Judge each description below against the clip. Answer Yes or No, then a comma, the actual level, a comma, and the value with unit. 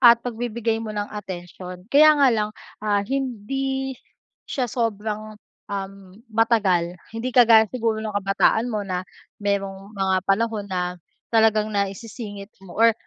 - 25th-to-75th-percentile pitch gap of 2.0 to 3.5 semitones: Yes, average, 2.8 semitones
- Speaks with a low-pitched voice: No, high, 215 Hz